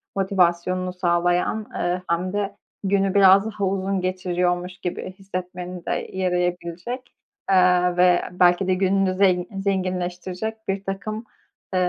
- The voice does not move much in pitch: Yes, narrow, 1.5 semitones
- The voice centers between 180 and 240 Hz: Yes, medium, 185 Hz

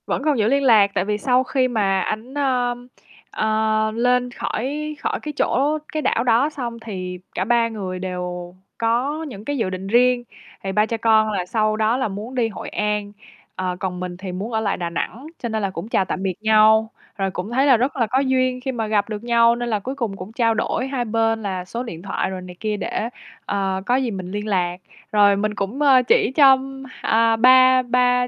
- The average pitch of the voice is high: Yes, high, 225 Hz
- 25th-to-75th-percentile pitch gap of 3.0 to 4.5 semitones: Yes, average, 4.0 semitones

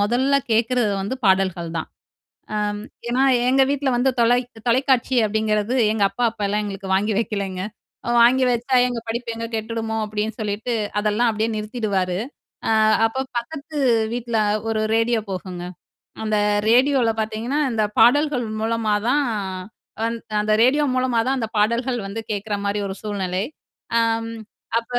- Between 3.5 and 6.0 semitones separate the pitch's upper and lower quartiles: No, average, 2.8 semitones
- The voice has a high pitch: Yes, high, 225 Hz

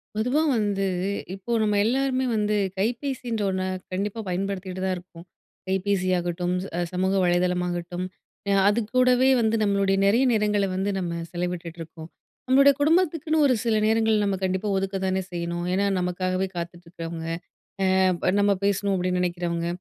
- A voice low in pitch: No, high, 195 Hz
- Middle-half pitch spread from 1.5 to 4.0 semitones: Yes, average, 3.5 semitones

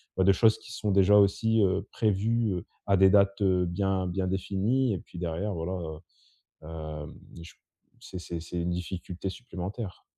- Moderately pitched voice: No, very low, 95 Hz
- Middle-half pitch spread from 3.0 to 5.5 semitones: No, narrow, 2.6 semitones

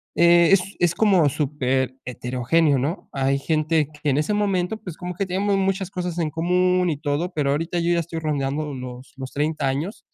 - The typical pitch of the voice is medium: Yes, medium, 160 Hz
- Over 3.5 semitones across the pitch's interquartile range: Yes, average, 4.2 semitones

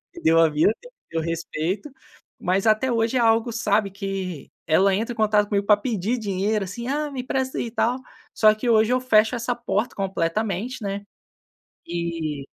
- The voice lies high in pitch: Yes, high, 210 Hz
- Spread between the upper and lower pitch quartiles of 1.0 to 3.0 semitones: No, average, 3.9 semitones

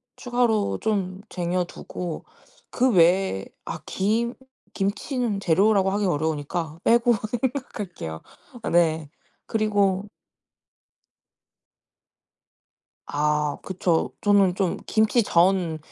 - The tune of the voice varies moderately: Yes, average, 4.2 semitones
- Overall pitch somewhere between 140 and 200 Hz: Yes, high, 195 Hz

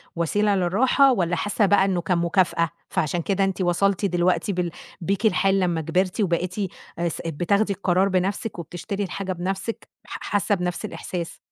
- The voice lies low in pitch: No, medium, 185 Hz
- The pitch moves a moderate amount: No, narrow, 2.3 semitones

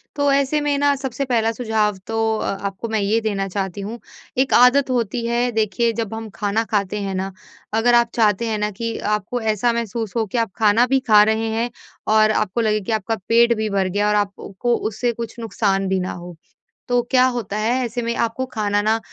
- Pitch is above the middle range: Yes, high, 225 Hz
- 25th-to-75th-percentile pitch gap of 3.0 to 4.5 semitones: No, narrow, 2.4 semitones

